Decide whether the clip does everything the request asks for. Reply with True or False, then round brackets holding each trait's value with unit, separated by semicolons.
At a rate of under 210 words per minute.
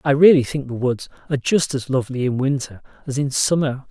False (215 wpm)